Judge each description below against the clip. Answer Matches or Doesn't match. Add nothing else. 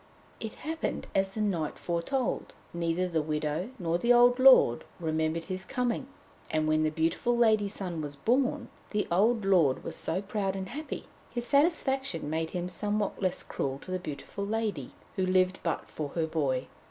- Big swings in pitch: Matches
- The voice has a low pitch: Doesn't match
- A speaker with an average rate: Matches